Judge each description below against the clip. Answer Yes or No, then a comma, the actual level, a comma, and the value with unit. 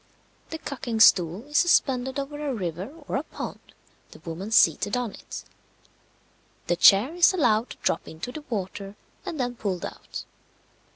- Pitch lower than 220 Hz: No, high, 235 Hz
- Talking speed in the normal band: Yes, average, 160 wpm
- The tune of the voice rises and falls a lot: Yes, wide, 6.2 semitones